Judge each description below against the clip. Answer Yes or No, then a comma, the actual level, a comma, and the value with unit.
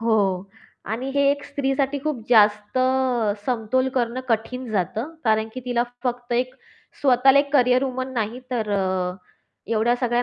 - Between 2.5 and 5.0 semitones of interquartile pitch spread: Yes, average, 2.8 semitones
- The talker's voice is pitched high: Yes, high, 245 Hz